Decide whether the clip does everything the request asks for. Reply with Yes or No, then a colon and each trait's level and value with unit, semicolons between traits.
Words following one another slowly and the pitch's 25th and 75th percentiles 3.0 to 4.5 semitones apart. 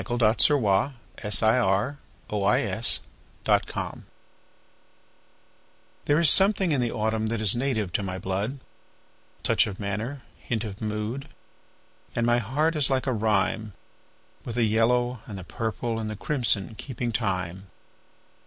Yes: slow, 125 wpm; average, 3.4 semitones